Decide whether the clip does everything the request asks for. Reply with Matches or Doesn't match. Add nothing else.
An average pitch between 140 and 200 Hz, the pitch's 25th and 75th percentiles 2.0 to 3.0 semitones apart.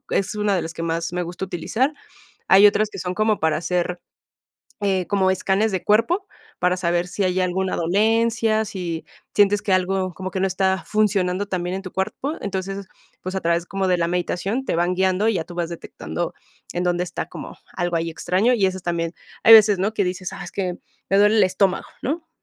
Matches